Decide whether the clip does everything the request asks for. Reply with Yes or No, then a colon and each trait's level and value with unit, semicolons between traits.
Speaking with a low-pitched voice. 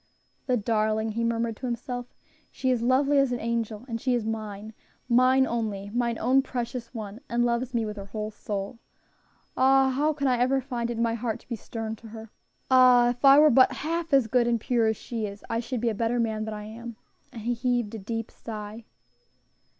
No: high, 235 Hz